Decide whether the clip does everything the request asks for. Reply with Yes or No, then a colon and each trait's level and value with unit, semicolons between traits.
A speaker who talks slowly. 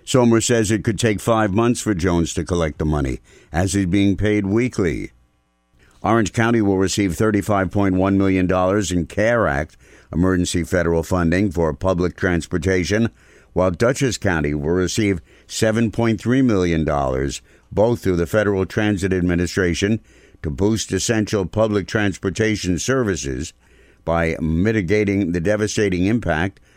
Yes: slow, 130 wpm